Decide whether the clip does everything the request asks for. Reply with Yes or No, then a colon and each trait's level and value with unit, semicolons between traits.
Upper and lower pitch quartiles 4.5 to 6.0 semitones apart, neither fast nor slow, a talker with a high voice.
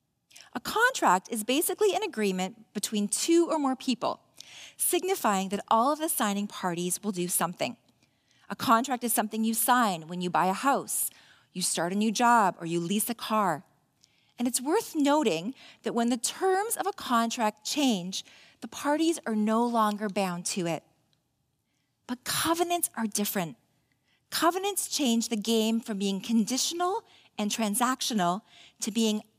Yes: average, 5.2 semitones; average, 155 wpm; high, 225 Hz